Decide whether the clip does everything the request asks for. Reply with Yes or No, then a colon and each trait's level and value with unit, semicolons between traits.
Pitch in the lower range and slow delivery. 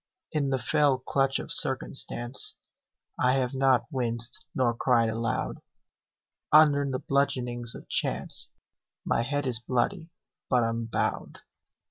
Yes: low, 130 Hz; slow, 120 wpm